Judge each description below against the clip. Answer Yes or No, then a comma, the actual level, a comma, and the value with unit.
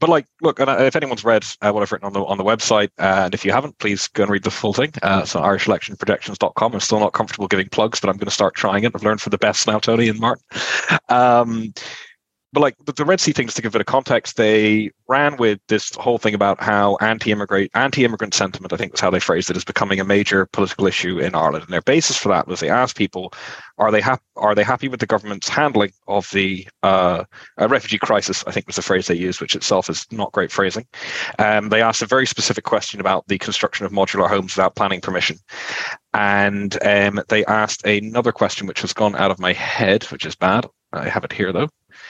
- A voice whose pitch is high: No, low, 105 Hz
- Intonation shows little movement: No, average, 3.2 semitones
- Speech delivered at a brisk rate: Yes, fast, 230 wpm